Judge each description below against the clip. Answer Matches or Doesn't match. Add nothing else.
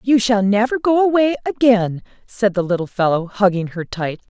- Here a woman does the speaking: Matches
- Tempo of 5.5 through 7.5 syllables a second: Doesn't match